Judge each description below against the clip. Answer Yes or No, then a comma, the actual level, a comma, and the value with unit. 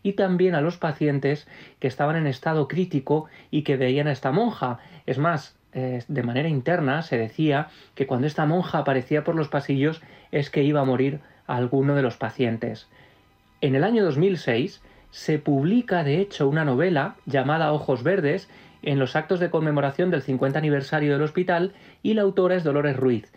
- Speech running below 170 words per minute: No, average, 180 wpm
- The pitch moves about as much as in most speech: Yes, average, 3.6 semitones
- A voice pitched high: No, medium, 145 Hz